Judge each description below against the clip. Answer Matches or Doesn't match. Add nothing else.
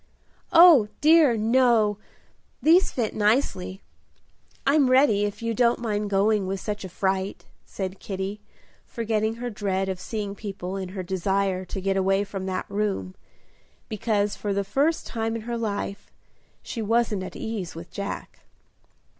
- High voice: Matches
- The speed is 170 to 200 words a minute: Doesn't match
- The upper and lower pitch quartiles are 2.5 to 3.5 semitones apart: Matches